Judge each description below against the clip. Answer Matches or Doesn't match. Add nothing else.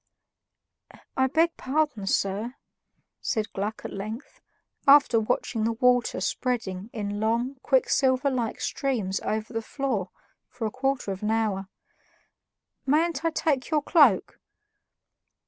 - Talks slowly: Matches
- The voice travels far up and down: Doesn't match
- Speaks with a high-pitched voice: Matches